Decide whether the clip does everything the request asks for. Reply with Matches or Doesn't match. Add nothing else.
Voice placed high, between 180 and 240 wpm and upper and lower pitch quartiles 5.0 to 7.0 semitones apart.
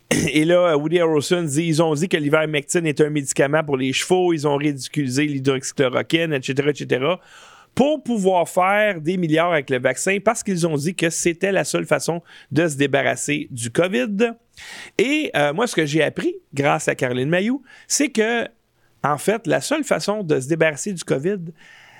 Doesn't match